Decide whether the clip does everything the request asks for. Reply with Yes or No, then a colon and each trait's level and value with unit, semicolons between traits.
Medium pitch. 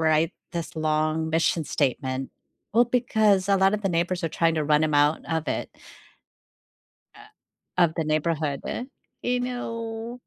Yes: medium, 165 Hz